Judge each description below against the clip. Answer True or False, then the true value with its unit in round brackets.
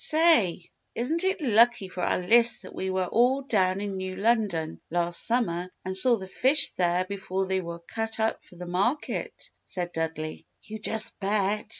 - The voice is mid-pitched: False (195 Hz)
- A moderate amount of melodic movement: True (4.5 semitones)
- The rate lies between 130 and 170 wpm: False (180 wpm)